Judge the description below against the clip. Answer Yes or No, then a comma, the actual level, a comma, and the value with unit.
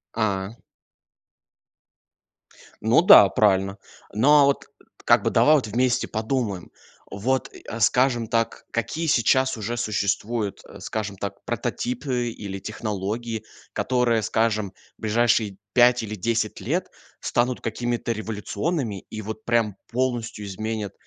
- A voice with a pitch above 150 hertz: No, low, 115 Hz